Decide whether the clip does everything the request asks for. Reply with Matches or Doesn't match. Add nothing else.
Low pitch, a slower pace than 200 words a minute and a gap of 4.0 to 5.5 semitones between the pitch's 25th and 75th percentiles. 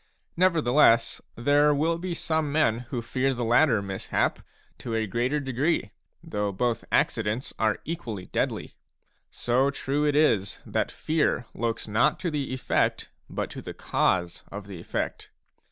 Matches